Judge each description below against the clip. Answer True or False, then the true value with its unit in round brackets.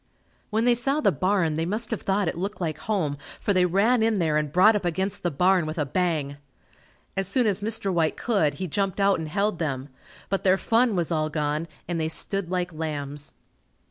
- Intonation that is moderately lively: True (4.4 semitones)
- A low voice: False (180 Hz)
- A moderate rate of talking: False (215 wpm)